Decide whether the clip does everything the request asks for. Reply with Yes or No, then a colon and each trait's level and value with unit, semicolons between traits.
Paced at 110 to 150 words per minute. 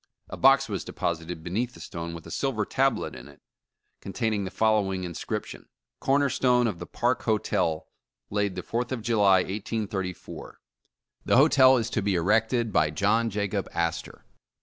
No: average, 170 wpm